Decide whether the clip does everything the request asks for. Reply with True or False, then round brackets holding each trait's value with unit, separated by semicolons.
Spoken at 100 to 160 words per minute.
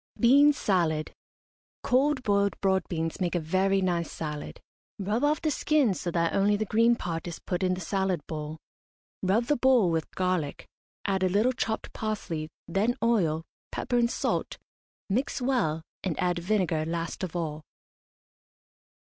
True (155 wpm)